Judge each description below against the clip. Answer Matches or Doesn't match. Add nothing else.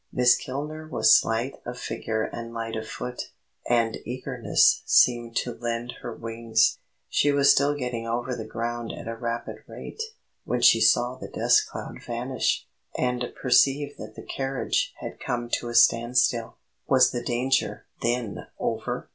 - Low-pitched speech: Matches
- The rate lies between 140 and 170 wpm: Matches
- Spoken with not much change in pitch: Matches